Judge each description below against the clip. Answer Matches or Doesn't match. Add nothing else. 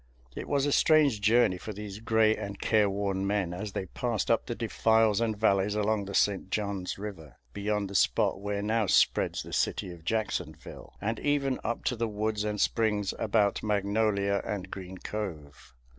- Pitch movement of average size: Doesn't match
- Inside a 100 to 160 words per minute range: Doesn't match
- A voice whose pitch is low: Matches